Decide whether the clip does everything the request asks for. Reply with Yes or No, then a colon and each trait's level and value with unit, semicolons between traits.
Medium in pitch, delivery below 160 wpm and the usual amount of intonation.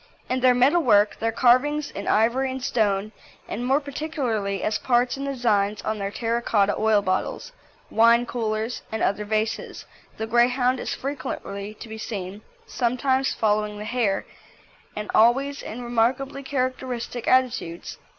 No: high, 235 Hz; average, 150 wpm; average, 3.3 semitones